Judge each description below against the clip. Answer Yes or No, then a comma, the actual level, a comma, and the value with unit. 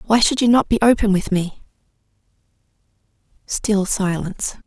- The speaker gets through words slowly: Yes, slow, 130 wpm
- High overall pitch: Yes, high, 205 Hz